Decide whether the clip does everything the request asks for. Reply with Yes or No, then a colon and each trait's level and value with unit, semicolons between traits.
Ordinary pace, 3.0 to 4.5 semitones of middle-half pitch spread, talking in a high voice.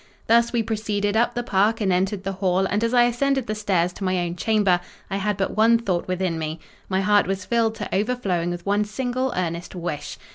No: fast, 220 wpm; average, 3.7 semitones; high, 205 Hz